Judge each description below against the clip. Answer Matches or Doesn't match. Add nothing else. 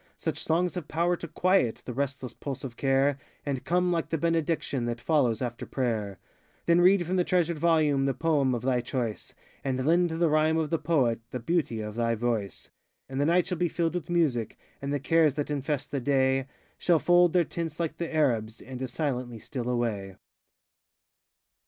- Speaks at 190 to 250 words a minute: Matches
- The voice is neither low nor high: Matches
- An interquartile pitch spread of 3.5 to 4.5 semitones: Doesn't match